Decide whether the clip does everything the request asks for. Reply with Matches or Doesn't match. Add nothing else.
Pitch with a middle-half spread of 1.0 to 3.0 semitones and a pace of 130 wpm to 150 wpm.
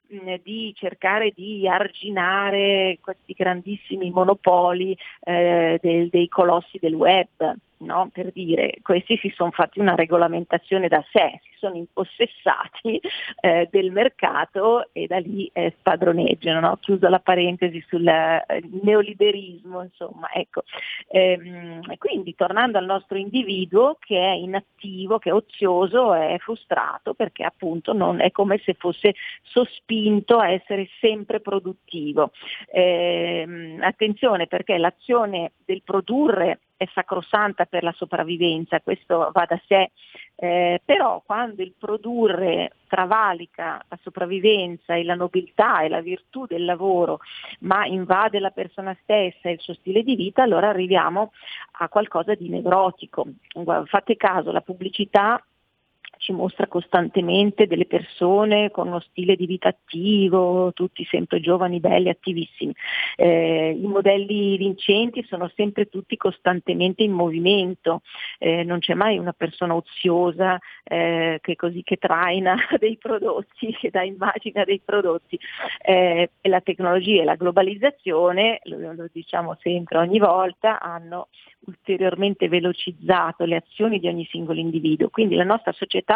Matches